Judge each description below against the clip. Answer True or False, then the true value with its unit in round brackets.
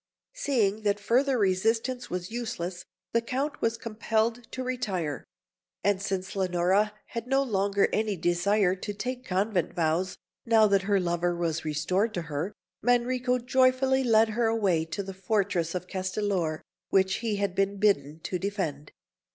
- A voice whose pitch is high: True (200 Hz)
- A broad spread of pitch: False (4.0 semitones)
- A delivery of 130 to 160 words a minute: True (150 wpm)